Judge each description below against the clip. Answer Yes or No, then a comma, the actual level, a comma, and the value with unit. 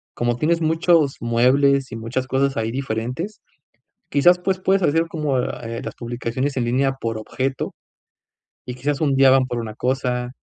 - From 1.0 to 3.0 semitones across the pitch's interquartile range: No, average, 3.4 semitones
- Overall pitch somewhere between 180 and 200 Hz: No, low, 135 Hz